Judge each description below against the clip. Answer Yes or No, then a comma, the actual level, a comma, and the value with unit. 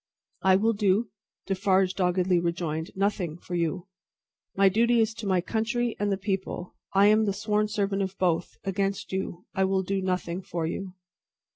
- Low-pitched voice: No, high, 195 Hz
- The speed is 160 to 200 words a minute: Yes, average, 170 wpm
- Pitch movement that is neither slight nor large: No, narrow, 2.3 semitones